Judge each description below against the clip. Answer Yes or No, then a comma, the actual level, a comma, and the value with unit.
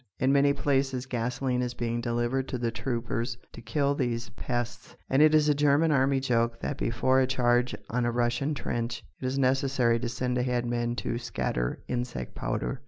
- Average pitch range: No, narrow, 2.1 semitones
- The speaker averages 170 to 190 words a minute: Yes, average, 185 wpm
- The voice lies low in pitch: Yes, low, 125 Hz